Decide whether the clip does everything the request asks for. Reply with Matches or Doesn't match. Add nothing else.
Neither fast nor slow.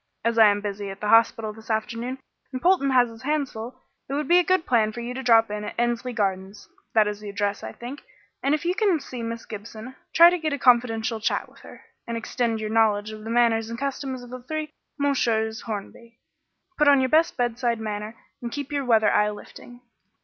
Doesn't match